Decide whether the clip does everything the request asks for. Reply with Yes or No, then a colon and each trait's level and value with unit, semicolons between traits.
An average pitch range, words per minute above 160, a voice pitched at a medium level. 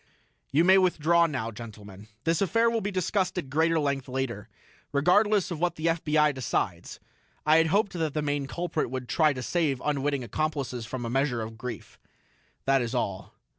Yes: average, 4.8 semitones; average, 180 wpm; medium, 150 Hz